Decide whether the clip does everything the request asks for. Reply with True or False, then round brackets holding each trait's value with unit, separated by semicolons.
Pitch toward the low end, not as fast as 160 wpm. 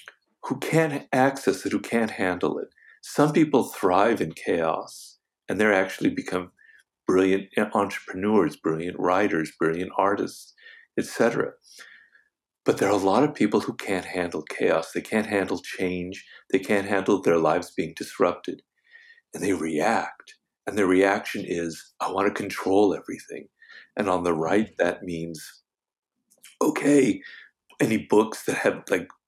True (100 Hz; 145 wpm)